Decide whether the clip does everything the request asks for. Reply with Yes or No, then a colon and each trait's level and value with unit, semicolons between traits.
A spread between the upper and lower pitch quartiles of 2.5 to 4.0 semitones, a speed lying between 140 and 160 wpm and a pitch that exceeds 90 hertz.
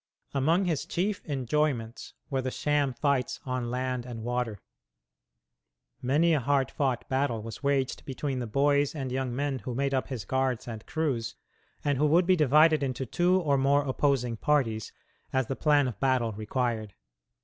No: average, 2.9 semitones; average, 170 wpm; low, 135 Hz